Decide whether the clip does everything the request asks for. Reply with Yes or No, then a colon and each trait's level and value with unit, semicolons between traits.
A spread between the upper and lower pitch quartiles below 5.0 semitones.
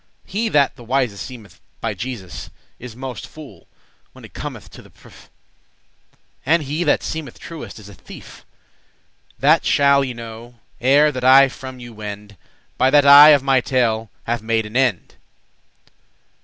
Yes: average, 3.8 semitones